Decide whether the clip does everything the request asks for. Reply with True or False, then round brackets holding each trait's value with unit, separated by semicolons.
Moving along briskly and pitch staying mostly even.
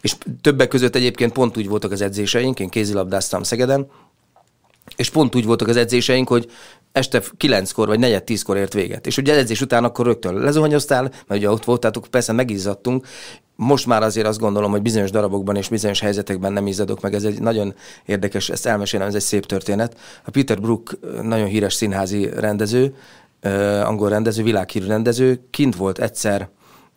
False (170 wpm; 3.3 semitones)